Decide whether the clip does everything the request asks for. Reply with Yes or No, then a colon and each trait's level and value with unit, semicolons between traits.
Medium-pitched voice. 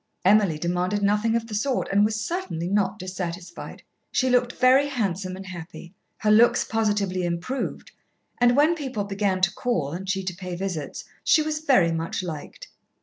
No: high, 200 Hz